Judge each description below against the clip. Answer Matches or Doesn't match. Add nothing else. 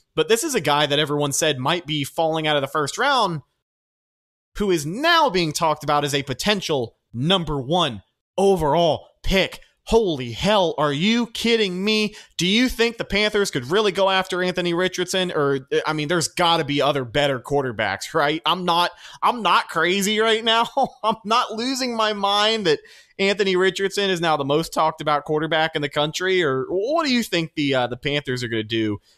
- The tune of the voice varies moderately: Doesn't match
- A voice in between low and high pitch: Matches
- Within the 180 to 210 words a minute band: Matches